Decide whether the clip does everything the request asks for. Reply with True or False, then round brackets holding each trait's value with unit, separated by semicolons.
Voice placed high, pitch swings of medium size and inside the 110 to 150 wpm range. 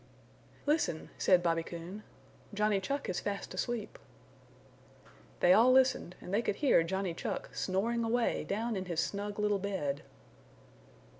True (200 Hz; 4.3 semitones; 140 wpm)